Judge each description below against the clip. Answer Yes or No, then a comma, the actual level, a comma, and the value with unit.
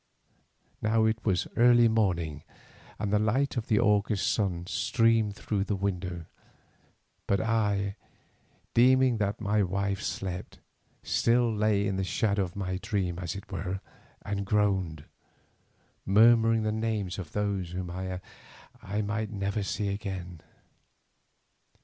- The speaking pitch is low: Yes, low, 100 Hz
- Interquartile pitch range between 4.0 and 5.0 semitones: No, narrow, 2.6 semitones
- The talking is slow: Yes, slow, 130 wpm